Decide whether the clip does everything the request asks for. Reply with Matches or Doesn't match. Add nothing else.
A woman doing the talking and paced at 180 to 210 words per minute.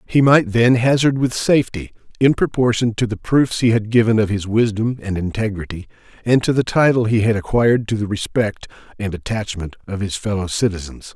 Doesn't match